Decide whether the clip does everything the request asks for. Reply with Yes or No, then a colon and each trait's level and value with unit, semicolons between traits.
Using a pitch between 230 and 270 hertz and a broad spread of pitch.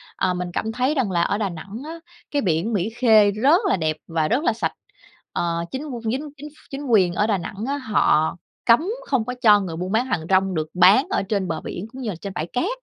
No: high, 210 Hz; wide, 6.4 semitones